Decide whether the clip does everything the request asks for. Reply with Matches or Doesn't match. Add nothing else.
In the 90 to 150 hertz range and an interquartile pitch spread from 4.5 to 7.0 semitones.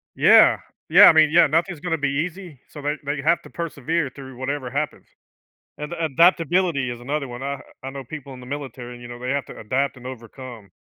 Doesn't match